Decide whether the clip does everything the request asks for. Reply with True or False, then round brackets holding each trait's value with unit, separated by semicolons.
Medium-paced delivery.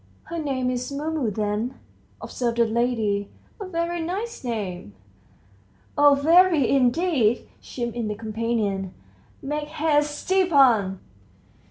False (110 wpm)